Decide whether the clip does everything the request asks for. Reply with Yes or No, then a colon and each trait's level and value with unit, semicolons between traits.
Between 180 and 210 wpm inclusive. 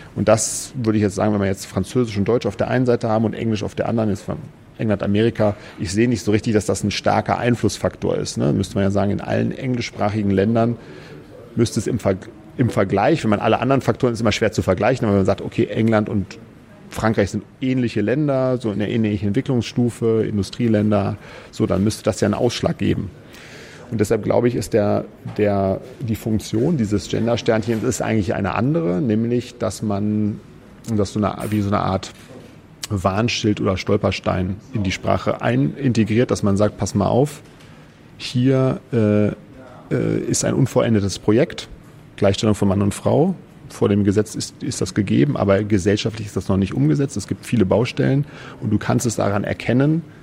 Yes: fast, 190 wpm